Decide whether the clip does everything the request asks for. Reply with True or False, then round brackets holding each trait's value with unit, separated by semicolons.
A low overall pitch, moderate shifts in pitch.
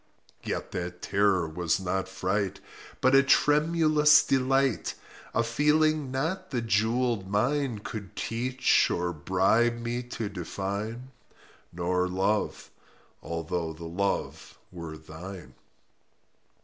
False (105 Hz; 6.1 semitones)